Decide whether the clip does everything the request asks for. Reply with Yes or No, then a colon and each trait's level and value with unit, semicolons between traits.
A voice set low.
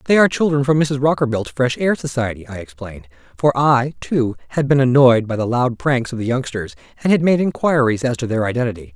Yes: low, 130 Hz